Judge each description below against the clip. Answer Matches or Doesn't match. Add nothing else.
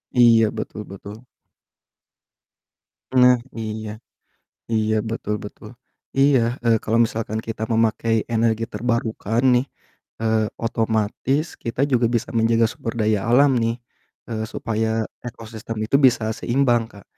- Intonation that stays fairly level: Matches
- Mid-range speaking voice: Doesn't match